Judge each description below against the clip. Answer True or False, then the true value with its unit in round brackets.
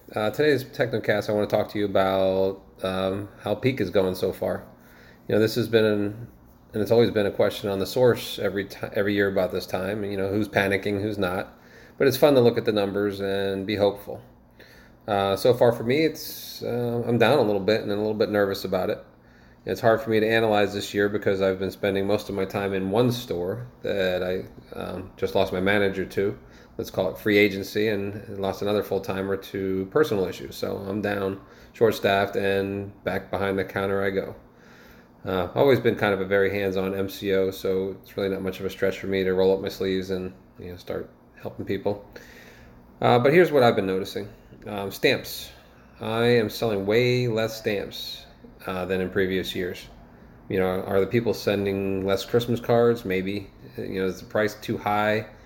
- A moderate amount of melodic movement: False (2.0 semitones)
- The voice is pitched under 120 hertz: True (100 Hz)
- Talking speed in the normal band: False (210 wpm)